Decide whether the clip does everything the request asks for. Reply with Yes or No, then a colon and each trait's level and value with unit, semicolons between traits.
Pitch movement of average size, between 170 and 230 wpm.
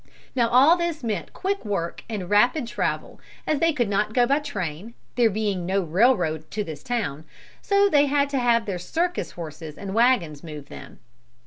No: wide, 7.6 semitones; average, 185 wpm